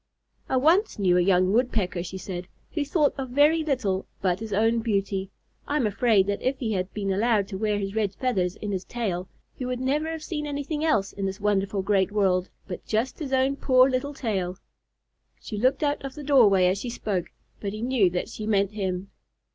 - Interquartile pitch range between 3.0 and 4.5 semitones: No, average, 5.3 semitones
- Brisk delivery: Yes, fast, 210 wpm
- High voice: Yes, high, 215 Hz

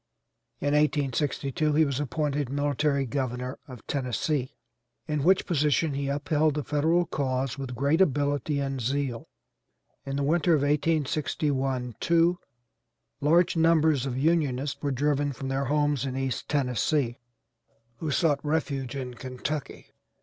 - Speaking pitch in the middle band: Yes, medium, 145 Hz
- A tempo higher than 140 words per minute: No, slow, 135 wpm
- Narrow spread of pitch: Yes, narrow, 2.2 semitones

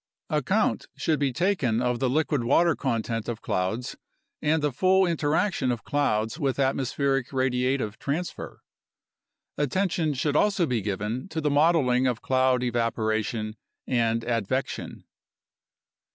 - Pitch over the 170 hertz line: No, low, 130 Hz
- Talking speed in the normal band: No, slow, 125 wpm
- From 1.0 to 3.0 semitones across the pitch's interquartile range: No, average, 4.2 semitones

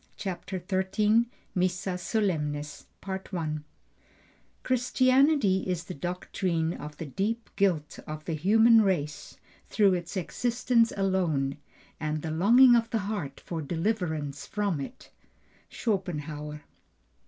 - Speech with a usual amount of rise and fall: No, wide, 5.7 semitones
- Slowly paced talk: Yes, slow, 110 wpm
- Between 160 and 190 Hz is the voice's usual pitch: Yes, medium, 185 Hz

